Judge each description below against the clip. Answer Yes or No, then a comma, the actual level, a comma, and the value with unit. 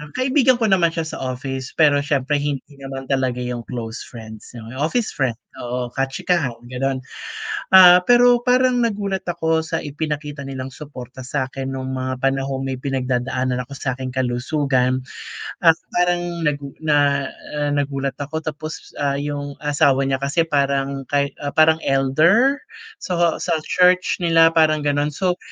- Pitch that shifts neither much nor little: Yes, average, 3.6 semitones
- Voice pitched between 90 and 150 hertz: Yes, medium, 140 Hz